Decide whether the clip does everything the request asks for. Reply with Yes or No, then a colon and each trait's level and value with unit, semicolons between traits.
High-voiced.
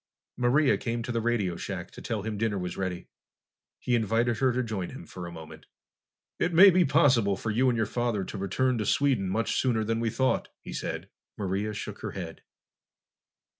No: low, 115 Hz